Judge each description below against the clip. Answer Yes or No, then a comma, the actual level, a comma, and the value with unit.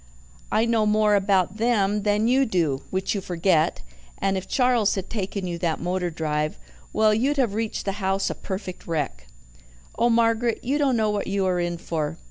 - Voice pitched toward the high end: Yes, high, 200 Hz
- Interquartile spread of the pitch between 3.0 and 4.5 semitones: Yes, average, 3.9 semitones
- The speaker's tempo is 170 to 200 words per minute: Yes, average, 190 wpm